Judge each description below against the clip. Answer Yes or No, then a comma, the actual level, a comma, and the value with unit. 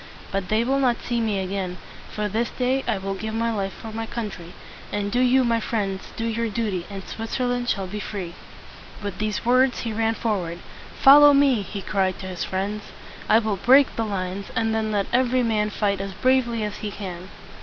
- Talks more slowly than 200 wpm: No, fast, 205 wpm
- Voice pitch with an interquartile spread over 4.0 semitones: No, average, 3.2 semitones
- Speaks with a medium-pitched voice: No, high, 215 Hz